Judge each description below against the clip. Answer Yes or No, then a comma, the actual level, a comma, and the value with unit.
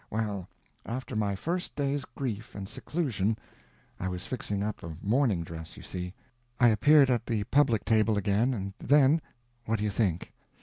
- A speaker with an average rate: Yes, average, 150 wpm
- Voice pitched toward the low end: Yes, low, 110 Hz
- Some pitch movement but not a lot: Yes, average, 4.4 semitones